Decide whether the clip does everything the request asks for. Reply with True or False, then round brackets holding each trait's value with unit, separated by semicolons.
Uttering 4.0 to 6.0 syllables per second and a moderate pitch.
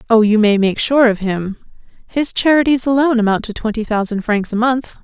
False (5.4 syllables/s; 230 Hz)